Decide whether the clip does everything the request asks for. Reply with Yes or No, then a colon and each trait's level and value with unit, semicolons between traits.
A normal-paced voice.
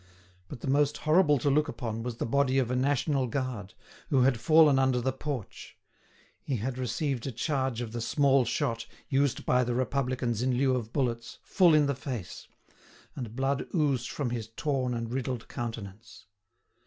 Yes: average, 180 wpm